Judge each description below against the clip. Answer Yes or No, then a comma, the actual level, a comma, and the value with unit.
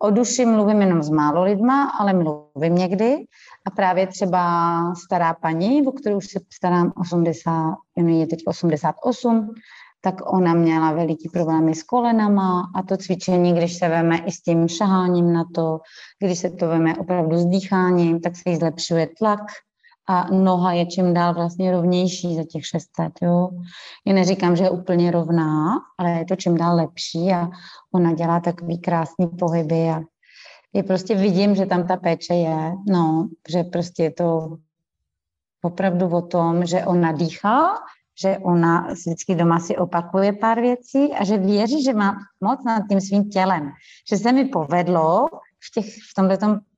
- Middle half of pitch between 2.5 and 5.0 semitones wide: Yes, average, 2.8 semitones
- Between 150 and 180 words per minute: Yes, average, 165 wpm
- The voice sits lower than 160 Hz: No, medium, 180 Hz